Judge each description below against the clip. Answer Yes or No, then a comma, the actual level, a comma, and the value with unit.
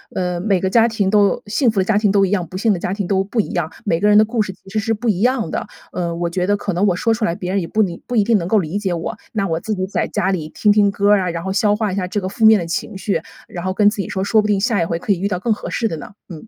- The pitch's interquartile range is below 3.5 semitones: Yes, average, 2.9 semitones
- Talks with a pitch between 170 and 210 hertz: Yes, high, 200 Hz